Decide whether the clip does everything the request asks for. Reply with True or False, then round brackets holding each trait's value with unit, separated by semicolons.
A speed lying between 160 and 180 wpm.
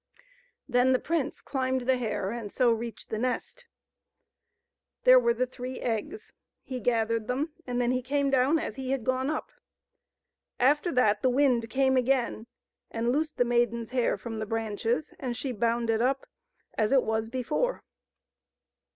True (165 wpm)